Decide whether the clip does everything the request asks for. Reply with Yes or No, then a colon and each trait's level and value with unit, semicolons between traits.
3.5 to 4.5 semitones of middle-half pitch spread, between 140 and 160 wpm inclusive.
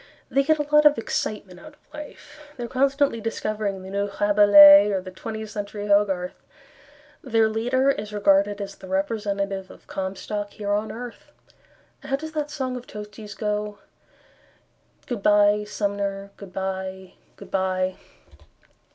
No: average, 2.7 semitones; average, 150 wpm